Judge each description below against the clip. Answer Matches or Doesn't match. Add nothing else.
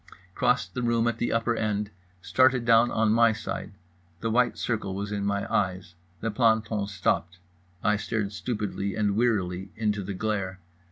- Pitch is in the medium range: Doesn't match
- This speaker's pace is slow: Doesn't match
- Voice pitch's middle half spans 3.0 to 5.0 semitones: Doesn't match